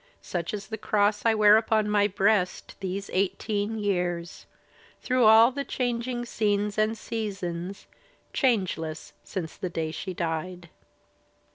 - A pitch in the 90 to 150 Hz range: No, high, 205 Hz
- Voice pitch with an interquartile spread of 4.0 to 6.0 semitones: No, average, 3.4 semitones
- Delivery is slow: Yes, slow, 130 wpm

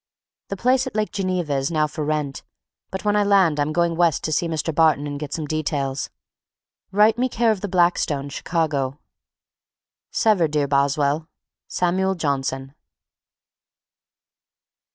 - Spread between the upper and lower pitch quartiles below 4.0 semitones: No, average, 4.8 semitones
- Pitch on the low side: No, medium, 160 Hz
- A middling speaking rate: Yes, average, 145 wpm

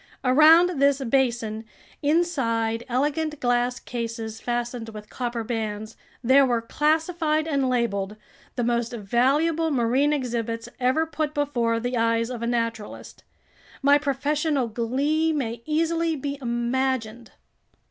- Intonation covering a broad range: No, average, 4.2 semitones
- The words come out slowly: Yes, slow, 120 wpm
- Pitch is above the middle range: Yes, very high, 250 Hz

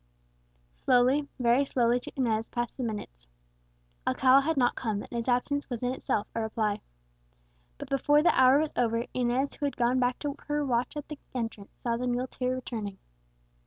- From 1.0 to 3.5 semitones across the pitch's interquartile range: Yes, narrow, 2.6 semitones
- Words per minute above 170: Yes, average, 180 wpm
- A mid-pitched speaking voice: No, very high, 250 Hz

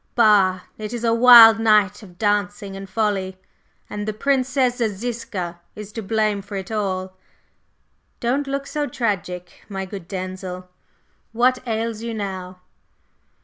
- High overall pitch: Yes, high, 210 Hz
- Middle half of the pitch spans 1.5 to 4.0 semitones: Yes, average, 3.4 semitones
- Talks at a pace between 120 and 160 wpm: Yes, average, 140 wpm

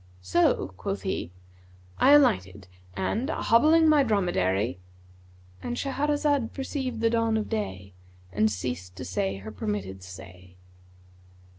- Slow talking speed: Yes, slow, 115 wpm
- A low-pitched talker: Yes, low, 105 Hz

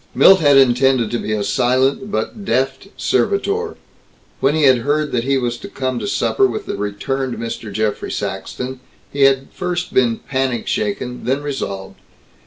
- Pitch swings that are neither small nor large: Yes, average, 3.2 semitones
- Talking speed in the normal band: Yes, average, 170 wpm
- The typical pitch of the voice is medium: No, low, 130 Hz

